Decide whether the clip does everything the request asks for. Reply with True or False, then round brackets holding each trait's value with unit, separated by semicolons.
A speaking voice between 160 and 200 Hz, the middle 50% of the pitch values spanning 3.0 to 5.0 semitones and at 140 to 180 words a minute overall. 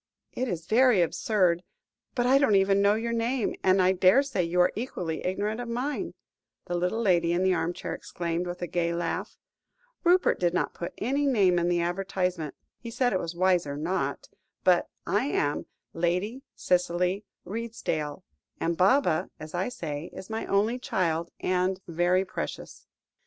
True (185 Hz; 4.3 semitones; 165 wpm)